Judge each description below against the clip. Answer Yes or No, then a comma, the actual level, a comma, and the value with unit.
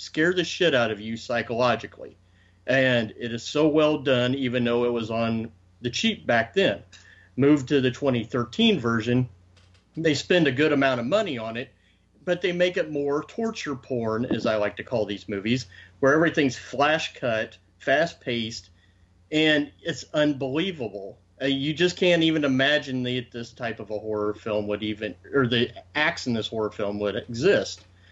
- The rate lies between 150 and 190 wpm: Yes, average, 175 wpm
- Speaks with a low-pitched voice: Yes, low, 120 Hz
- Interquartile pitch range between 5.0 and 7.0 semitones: Yes, wide, 5.4 semitones